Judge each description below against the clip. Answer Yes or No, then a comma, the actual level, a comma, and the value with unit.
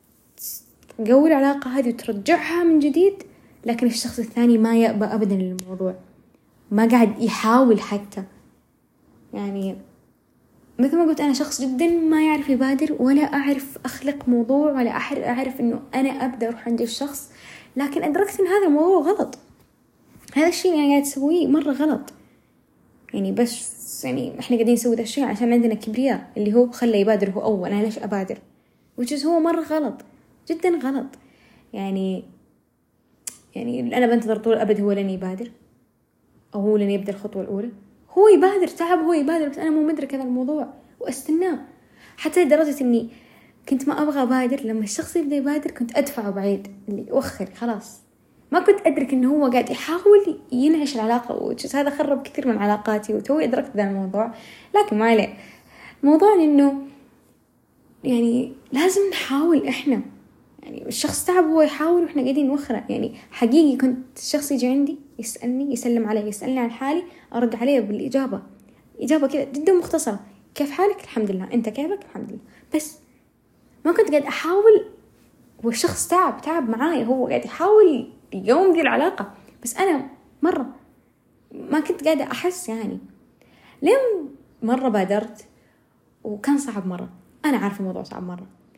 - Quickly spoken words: Yes, fast, 150 wpm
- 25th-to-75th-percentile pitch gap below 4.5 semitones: No, average, 4.9 semitones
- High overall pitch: Yes, very high, 265 Hz